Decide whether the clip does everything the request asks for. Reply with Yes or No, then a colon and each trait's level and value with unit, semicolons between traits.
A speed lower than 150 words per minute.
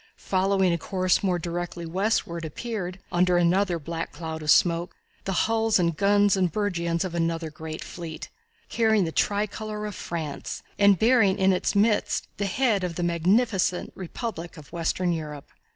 No: average, 165 wpm